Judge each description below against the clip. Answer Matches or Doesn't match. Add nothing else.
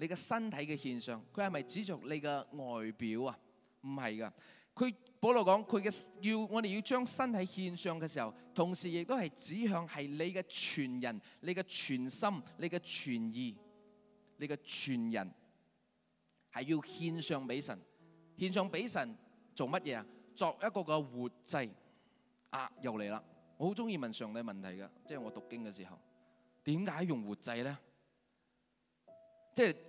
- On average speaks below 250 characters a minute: Matches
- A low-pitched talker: Doesn't match